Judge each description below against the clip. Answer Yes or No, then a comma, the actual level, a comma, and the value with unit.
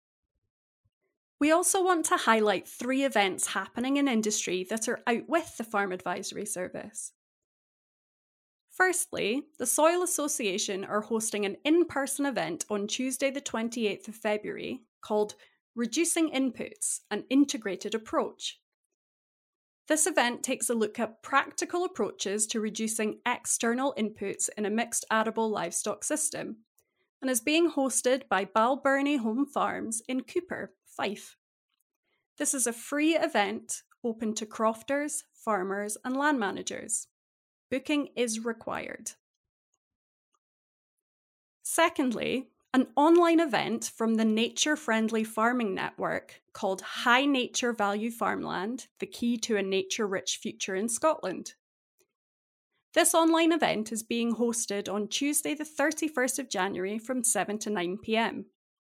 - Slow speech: Yes, slow, 125 wpm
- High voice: Yes, high, 240 Hz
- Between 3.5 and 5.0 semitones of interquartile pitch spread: No, wide, 5.5 semitones